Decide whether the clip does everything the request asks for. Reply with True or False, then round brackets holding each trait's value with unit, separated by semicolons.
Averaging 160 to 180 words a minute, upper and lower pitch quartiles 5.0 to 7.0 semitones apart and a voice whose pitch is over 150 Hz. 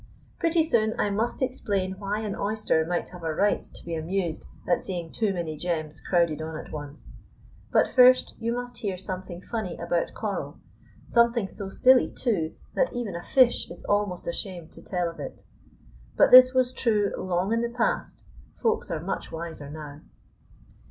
True (175 wpm; 5.5 semitones; 190 Hz)